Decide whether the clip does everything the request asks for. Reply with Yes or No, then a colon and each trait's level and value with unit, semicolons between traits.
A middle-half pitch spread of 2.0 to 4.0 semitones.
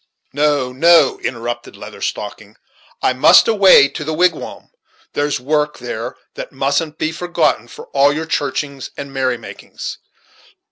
Yes: average, 3.4 semitones